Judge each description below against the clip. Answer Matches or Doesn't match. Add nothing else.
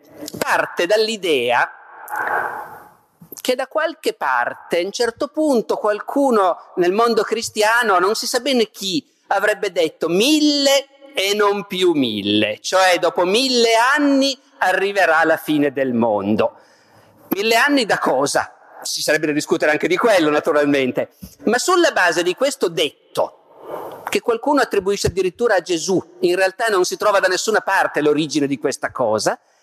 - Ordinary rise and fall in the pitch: Doesn't match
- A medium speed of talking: Matches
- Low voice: Doesn't match